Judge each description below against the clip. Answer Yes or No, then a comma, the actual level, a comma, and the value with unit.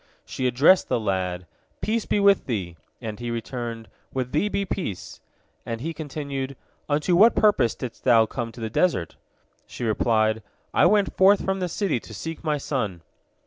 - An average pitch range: No, wide, 7.6 semitones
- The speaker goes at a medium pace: Yes, average, 175 wpm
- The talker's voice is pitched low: Yes, low, 130 Hz